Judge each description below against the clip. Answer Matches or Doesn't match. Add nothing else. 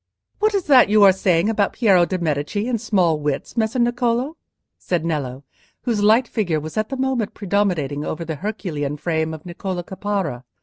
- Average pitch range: Doesn't match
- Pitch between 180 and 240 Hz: Matches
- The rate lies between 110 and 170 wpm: Doesn't match